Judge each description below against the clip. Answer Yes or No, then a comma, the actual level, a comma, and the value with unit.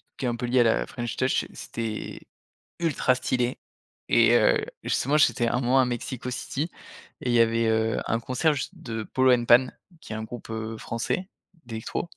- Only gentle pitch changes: Yes, narrow, 2.2 semitones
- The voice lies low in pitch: Yes, low, 120 Hz